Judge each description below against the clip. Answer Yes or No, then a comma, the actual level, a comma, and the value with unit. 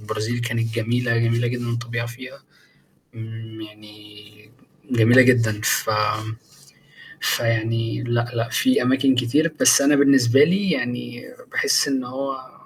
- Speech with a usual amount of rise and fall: No, narrow, 2.3 semitones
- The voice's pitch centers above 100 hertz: Yes, low, 120 Hz